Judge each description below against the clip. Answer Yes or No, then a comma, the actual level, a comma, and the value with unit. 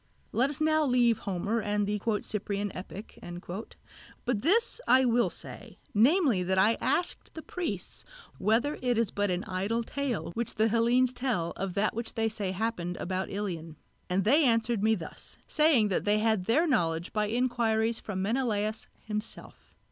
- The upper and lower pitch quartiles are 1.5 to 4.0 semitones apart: Yes, average, 3.7 semitones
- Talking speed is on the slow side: No, average, 165 wpm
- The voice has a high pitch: Yes, high, 220 Hz